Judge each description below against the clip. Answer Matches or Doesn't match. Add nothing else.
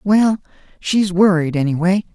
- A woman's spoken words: Doesn't match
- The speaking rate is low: Matches